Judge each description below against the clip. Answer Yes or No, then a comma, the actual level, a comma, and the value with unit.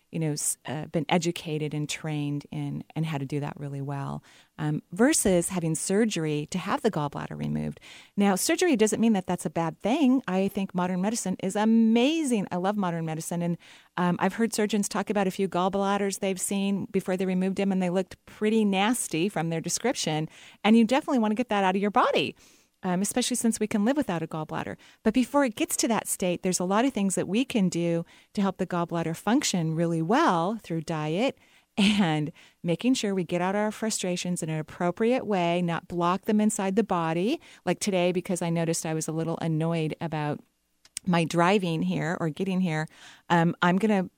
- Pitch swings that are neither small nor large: Yes, average, 4.3 semitones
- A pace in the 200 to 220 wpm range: Yes, fast, 205 wpm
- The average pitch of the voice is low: No, medium, 185 Hz